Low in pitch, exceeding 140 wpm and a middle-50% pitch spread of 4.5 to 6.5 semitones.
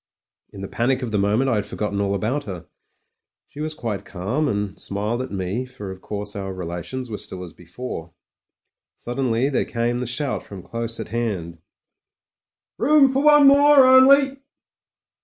Yes: low, 115 Hz; average, 170 wpm; wide, 5.6 semitones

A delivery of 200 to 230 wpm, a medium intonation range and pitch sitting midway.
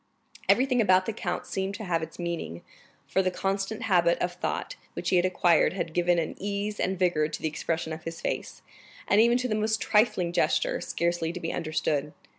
Yes: fast, 205 wpm; average, 3.5 semitones; medium, 180 Hz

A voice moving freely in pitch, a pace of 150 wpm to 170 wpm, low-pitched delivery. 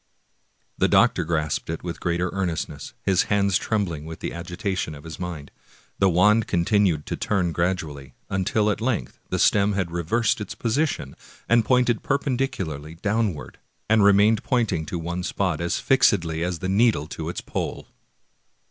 No: average, 4.2 semitones; average, 160 wpm; very low, 95 Hz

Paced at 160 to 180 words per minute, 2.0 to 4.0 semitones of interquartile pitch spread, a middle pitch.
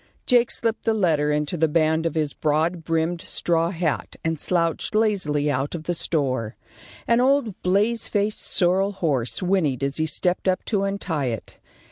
No: average, 170 wpm; average, 4.6 semitones; medium, 165 Hz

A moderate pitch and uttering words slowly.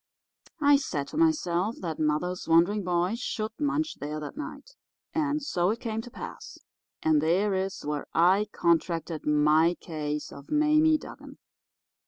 No: medium, 180 Hz; average, 150 wpm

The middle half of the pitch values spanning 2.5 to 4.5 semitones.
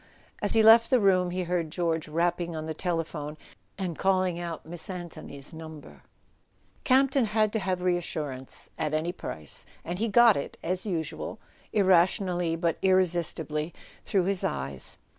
Yes: average, 3.1 semitones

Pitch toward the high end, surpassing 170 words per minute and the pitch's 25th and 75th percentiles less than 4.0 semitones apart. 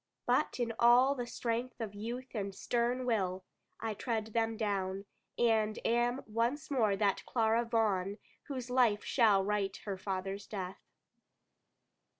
No: high, 225 Hz; average, 140 wpm; average, 3.1 semitones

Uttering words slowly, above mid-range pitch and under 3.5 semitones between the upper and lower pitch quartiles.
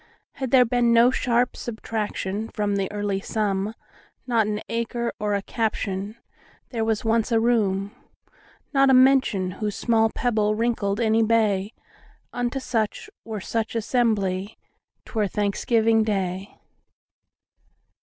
Yes: slow, 105 wpm; high, 220 Hz; narrow, 2.4 semitones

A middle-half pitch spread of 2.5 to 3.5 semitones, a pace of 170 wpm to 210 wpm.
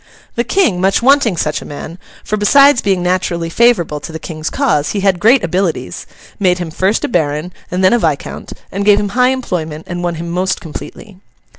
No: average, 4.3 semitones; average, 190 wpm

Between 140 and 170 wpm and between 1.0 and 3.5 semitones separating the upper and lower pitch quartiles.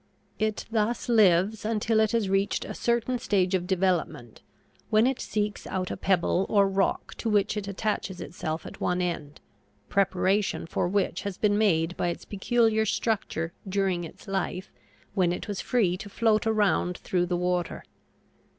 Yes: average, 165 wpm; average, 3.2 semitones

